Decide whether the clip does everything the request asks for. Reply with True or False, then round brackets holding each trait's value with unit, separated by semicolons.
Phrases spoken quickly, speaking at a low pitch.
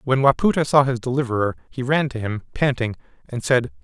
False (190 wpm; 130 Hz)